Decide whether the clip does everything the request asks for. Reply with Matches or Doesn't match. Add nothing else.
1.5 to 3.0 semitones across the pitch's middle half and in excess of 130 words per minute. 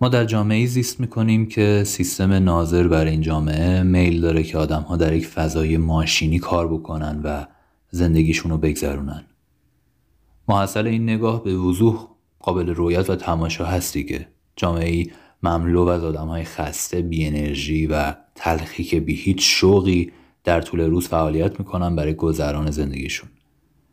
Matches